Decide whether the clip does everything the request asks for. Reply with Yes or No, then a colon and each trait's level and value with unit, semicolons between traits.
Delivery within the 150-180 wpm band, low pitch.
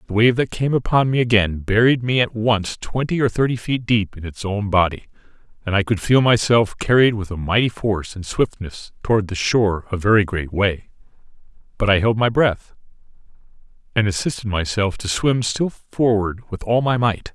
No: average, 190 wpm; low, 110 Hz